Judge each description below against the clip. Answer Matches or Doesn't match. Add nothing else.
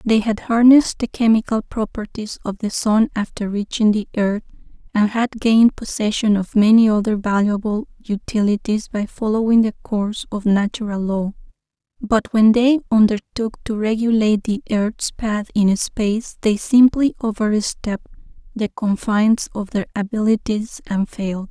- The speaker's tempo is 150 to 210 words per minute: Doesn't match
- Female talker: Matches